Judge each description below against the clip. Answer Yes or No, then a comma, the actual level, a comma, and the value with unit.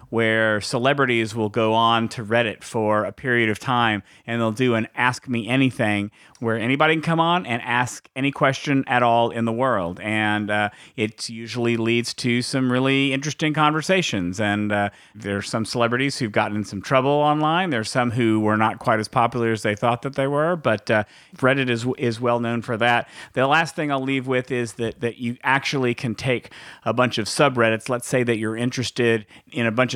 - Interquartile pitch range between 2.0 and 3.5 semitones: Yes, average, 3.0 semitones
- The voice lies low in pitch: Yes, low, 120 Hz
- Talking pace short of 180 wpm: No, fast, 205 wpm